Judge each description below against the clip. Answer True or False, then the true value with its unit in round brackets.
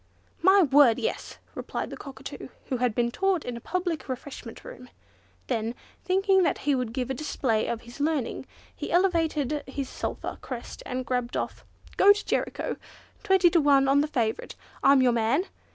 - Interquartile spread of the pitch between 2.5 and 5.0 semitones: False (5.4 semitones)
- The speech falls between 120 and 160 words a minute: False (175 wpm)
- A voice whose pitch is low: False (275 Hz)